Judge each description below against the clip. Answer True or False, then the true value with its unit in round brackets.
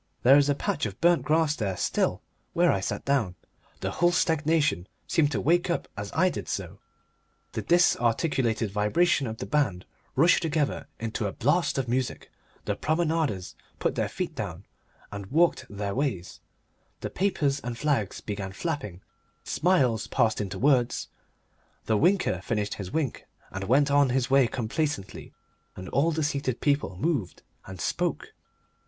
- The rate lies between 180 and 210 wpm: False (160 wpm)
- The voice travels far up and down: True (7.0 semitones)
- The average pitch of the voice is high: False (135 Hz)